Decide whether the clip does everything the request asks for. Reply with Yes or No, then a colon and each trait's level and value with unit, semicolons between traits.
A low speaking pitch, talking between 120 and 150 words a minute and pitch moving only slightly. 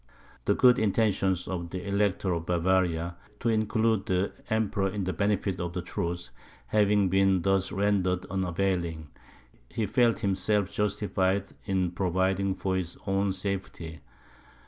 Yes: very low, 95 Hz; slow, 135 wpm; narrow, 2.1 semitones